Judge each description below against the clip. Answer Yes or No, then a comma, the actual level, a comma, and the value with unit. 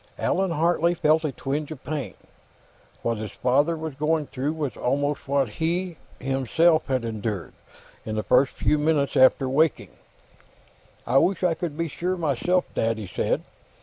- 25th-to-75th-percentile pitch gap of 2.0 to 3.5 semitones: No, average, 3.9 semitones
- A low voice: No, medium, 145 Hz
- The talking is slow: No, average, 160 wpm